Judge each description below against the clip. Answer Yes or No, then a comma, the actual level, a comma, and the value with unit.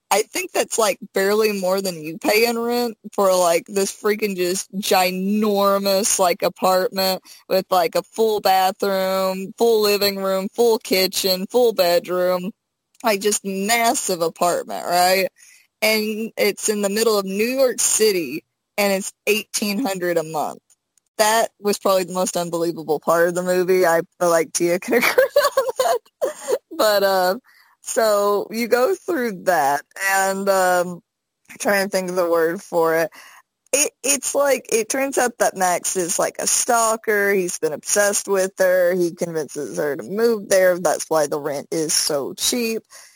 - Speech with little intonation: No, average, 3.6 semitones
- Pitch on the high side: Yes, high, 195 Hz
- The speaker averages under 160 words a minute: No, average, 165 wpm